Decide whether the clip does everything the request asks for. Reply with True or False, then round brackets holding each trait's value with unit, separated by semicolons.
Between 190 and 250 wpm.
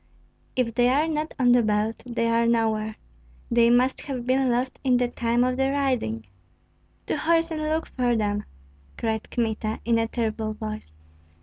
False (175 wpm)